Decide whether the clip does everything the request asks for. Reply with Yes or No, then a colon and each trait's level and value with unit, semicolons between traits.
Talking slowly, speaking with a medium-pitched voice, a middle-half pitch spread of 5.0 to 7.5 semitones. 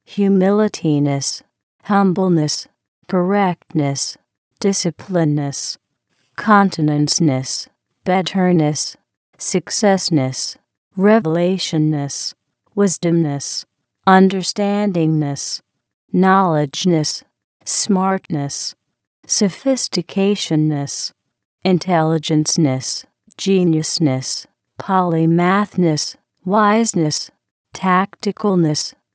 No: slow, 35 wpm; medium, 175 Hz; average, 4.1 semitones